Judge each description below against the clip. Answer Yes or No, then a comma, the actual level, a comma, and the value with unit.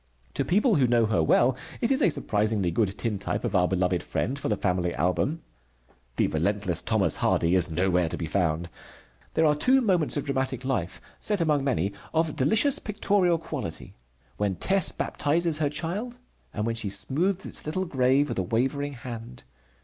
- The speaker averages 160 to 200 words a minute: Yes, average, 180 wpm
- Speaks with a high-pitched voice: No, low, 130 Hz